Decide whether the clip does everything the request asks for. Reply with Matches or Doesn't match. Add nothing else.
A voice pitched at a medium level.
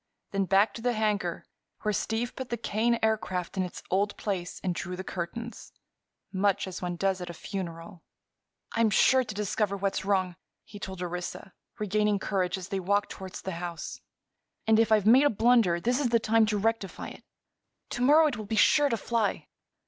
Doesn't match